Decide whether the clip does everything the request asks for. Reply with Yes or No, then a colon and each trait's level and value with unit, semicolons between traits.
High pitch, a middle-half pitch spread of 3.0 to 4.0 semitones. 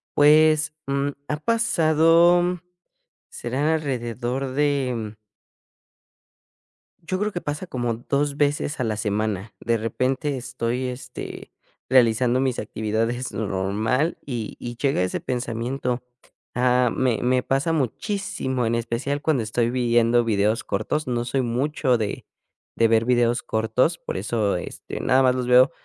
No: low, 125 Hz; average, 3.7 semitones